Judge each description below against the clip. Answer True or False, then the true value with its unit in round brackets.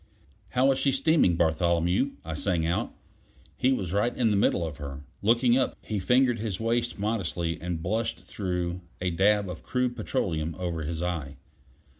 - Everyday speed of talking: True (170 wpm)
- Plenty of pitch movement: True (5.9 semitones)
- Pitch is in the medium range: False (95 Hz)